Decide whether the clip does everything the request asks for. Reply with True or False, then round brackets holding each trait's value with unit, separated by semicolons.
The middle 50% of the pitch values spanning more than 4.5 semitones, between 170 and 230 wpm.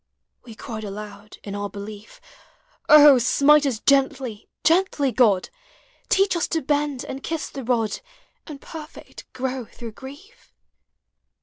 False (5.5 semitones; 135 wpm)